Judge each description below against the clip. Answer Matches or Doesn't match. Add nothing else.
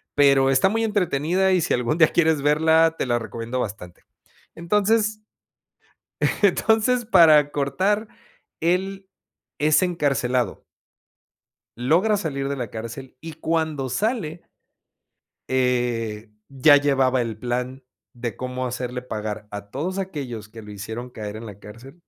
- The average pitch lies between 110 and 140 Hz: Matches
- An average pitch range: Doesn't match